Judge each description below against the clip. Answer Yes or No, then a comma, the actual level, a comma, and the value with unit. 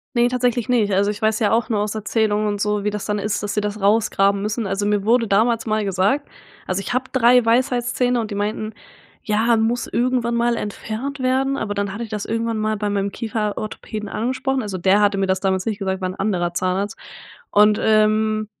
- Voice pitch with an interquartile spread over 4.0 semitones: No, narrow, 2.4 semitones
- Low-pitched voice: No, high, 215 Hz